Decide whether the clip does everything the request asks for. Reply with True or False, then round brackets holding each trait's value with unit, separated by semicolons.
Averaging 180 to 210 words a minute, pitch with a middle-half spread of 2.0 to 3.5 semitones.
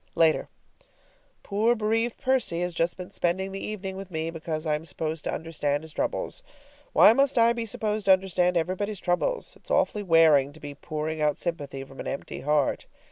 False (190 wpm; 4.8 semitones)